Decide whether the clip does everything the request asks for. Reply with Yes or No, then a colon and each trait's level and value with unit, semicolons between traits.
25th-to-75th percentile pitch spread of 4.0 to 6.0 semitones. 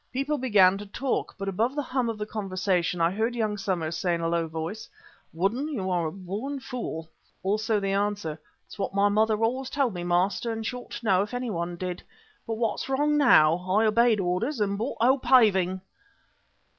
Yes: average, 4.6 semitones